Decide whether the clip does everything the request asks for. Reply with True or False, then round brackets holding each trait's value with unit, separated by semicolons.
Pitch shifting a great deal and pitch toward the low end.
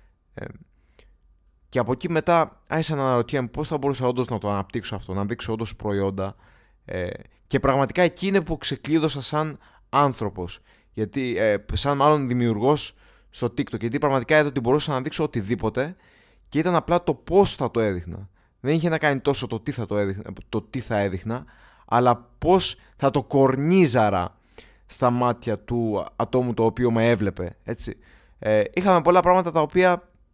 True (5.8 semitones; 125 Hz)